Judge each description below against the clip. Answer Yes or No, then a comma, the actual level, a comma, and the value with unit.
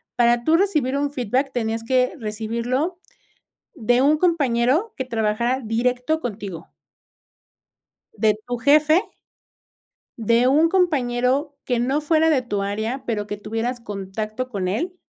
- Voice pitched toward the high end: Yes, high, 245 Hz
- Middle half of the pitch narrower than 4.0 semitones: No, average, 4.3 semitones